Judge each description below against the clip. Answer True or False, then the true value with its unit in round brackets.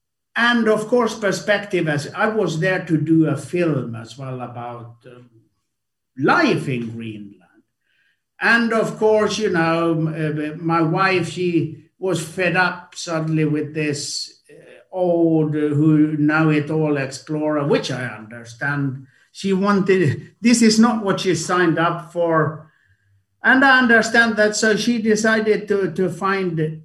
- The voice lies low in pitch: False (165 Hz)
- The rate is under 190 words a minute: True (145 wpm)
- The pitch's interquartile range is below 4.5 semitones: False (5.2 semitones)